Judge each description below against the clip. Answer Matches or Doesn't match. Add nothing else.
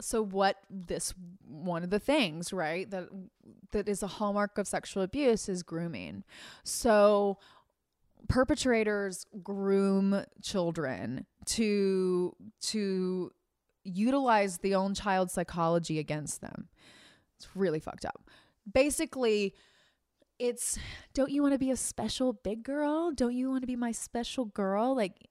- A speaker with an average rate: Doesn't match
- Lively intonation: Doesn't match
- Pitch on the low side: Doesn't match